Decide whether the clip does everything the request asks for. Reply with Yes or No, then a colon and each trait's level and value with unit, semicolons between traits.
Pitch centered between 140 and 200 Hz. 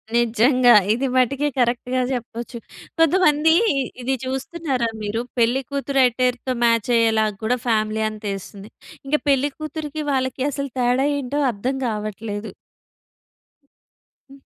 No: very high, 250 Hz